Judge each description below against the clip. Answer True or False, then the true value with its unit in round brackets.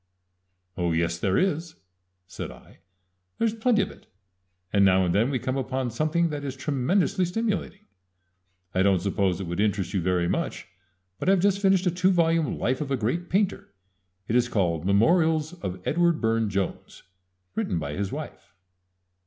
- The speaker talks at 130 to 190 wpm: True (175 wpm)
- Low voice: True (130 Hz)